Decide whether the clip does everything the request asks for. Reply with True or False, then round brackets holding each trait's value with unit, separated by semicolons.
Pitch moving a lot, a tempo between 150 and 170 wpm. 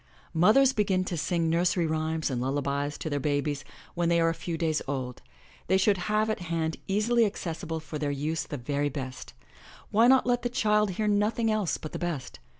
False (5.9 semitones; 200 wpm)